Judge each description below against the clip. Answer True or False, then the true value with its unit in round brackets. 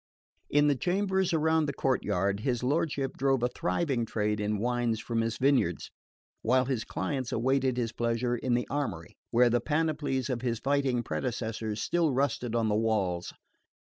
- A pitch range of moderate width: True (3.6 semitones)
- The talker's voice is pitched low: True (125 Hz)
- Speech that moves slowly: False (165 wpm)